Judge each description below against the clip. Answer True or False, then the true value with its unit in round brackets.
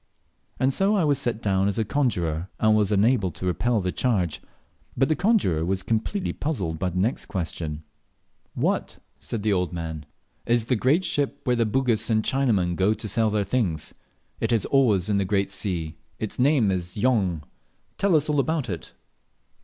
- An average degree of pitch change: False (5.9 semitones)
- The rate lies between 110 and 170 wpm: False (185 wpm)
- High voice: False (110 Hz)